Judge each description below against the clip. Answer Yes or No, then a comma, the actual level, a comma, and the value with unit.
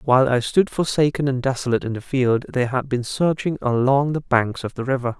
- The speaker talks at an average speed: No, fast, 220 wpm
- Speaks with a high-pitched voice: No, low, 130 Hz